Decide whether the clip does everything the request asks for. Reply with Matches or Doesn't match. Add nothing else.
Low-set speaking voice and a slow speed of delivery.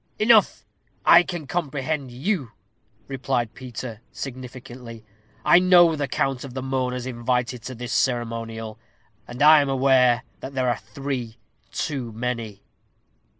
Matches